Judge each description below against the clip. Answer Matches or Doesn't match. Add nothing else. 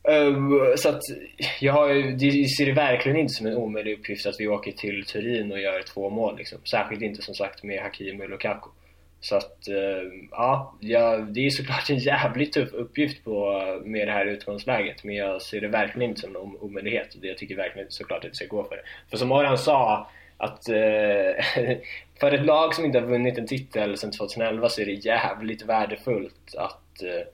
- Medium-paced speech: Doesn't match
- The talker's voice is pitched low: Matches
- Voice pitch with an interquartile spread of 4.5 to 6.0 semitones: Matches